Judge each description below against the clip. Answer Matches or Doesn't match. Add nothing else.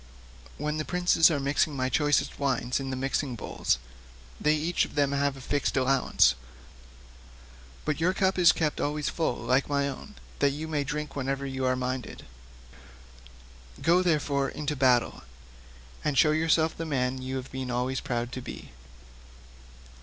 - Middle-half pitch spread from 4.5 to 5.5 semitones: Doesn't match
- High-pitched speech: Doesn't match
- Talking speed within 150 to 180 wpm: Matches